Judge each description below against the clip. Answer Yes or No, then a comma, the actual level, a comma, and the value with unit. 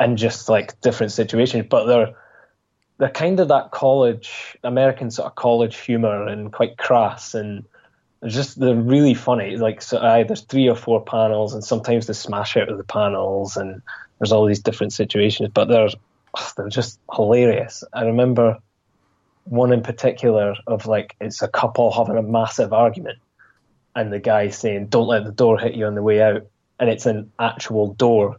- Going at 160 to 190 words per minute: Yes, average, 180 wpm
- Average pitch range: No, narrow, 2.2 semitones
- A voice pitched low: Yes, low, 110 Hz